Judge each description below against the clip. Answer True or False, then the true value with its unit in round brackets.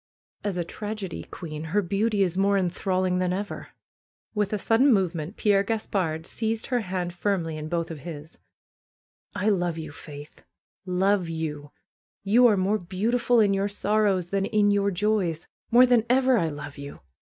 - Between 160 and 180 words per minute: True (165 wpm)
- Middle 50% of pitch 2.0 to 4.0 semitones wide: True (3.7 semitones)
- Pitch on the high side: True (195 Hz)